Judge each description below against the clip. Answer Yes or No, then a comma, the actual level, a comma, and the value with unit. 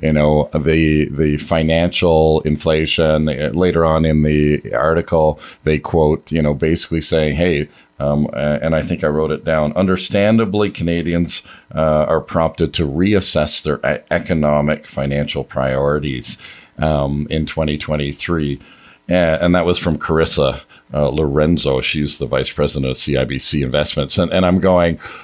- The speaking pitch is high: No, very low, 75 Hz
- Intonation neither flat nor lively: No, narrow, 2.0 semitones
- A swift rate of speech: No, average, 140 wpm